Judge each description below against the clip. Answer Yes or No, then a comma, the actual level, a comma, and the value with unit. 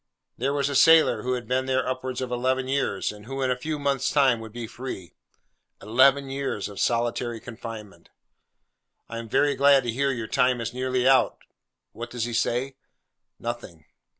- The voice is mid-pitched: No, low, 125 Hz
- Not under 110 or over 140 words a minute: No, average, 180 wpm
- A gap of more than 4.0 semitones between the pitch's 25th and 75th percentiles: No, narrow, 2.5 semitones